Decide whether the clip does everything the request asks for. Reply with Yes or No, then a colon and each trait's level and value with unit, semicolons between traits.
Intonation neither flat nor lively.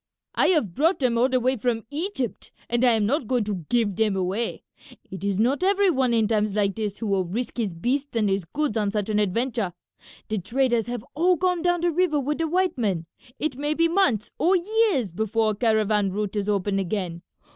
No: wide, 6.1 semitones